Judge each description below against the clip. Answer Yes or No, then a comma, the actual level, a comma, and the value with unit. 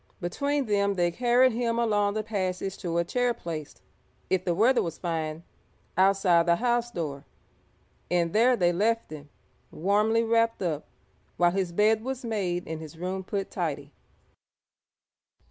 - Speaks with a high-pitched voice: Yes, high, 195 Hz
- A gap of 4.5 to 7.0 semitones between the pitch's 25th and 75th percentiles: Yes, average, 5.0 semitones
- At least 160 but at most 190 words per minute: No, average, 150 wpm